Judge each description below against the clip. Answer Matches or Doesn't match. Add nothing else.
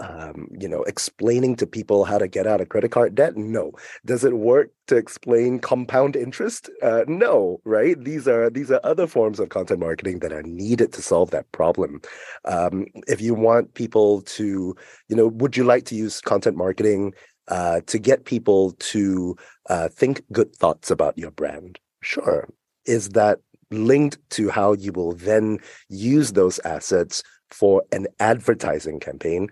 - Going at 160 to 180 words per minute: Matches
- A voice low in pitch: Matches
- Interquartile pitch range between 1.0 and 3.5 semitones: Doesn't match